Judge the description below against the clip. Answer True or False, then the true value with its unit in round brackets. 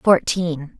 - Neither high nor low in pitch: True (170 Hz)